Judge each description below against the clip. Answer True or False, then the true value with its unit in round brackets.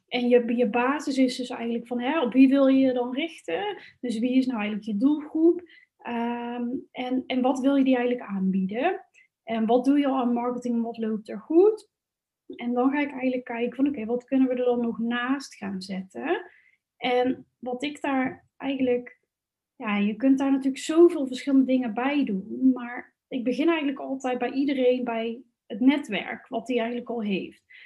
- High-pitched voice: True (255 Hz)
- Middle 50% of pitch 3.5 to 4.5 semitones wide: False (2.5 semitones)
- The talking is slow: False (195 wpm)